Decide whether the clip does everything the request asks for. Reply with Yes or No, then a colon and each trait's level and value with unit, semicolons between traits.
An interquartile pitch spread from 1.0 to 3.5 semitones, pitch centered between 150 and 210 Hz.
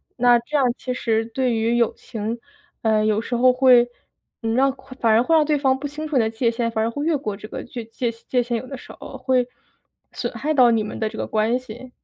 No: narrow, 2.5 semitones; high, 240 Hz